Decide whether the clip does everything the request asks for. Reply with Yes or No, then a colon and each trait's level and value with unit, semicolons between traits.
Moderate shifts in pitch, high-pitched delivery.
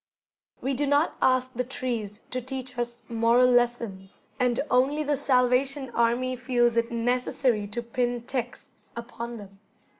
No: narrow, 1.5 semitones; high, 245 Hz